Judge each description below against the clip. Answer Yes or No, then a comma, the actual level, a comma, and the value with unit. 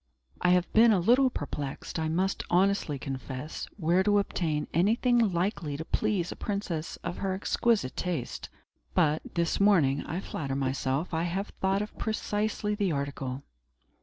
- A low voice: No, medium, 175 Hz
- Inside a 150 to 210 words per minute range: Yes, average, 155 wpm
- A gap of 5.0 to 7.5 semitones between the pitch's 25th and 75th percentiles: Yes, wide, 5.4 semitones